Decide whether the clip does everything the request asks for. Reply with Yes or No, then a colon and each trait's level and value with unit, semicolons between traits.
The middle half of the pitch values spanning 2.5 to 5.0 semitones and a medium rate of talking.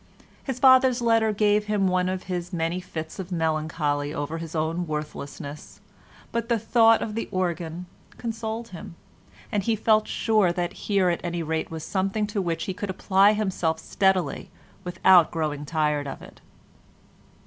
Yes: average, 4.6 semitones; average, 160 wpm